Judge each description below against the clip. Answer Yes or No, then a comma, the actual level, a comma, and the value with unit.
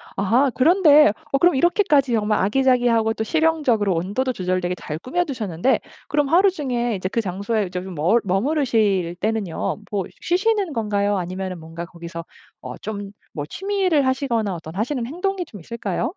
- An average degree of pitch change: No, wide, 7.2 semitones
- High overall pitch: Yes, high, 225 Hz